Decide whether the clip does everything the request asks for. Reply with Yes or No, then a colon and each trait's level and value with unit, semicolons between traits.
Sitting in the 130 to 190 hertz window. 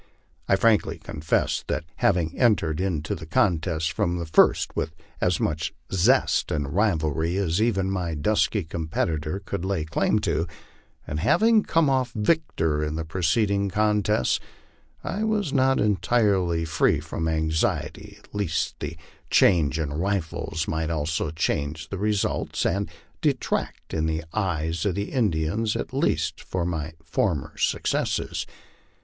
No: very low, 85 Hz